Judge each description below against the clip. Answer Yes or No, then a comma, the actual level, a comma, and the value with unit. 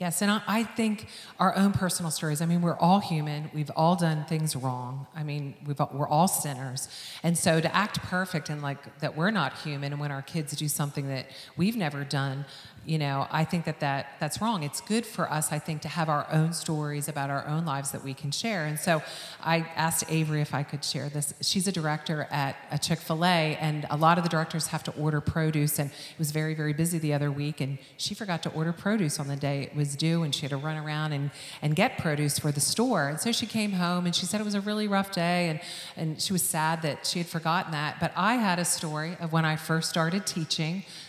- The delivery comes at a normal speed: No, fast, 245 wpm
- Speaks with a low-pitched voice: No, medium, 155 Hz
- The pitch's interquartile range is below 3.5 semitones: Yes, average, 2.7 semitones